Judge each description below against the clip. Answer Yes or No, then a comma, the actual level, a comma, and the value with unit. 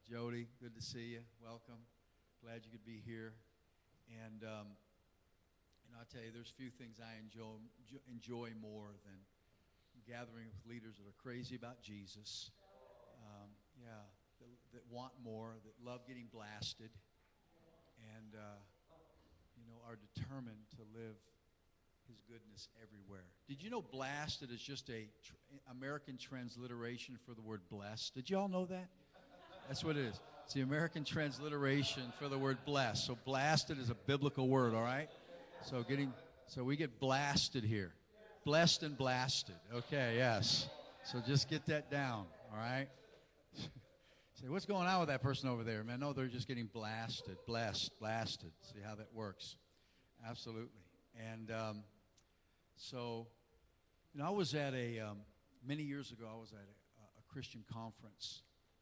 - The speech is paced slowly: No, average, 160 wpm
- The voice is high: No, low, 115 Hz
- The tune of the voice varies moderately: Yes, average, 3.7 semitones